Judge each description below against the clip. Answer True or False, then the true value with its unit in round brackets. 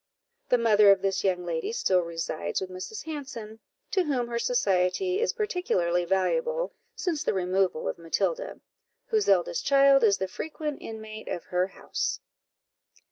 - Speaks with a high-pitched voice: True (220 Hz)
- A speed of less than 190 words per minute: True (150 wpm)